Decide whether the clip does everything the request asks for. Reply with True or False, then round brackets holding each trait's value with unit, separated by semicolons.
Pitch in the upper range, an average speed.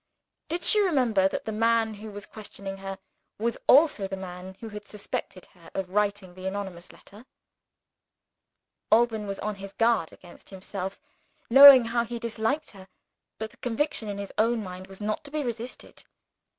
True (210 Hz; 170 wpm)